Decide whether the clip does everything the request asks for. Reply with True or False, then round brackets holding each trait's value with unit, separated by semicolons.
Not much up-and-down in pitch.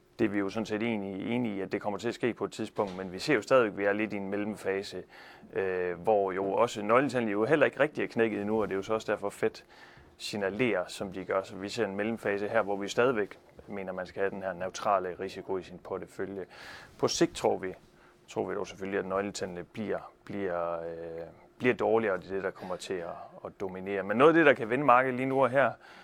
True (2.2 semitones)